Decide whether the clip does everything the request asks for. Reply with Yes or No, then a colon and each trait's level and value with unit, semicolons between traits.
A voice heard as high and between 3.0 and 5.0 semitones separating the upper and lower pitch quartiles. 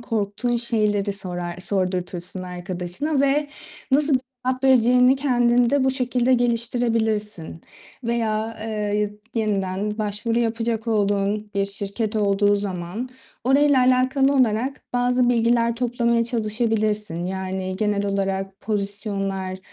Yes: high, 220 Hz; average, 3.6 semitones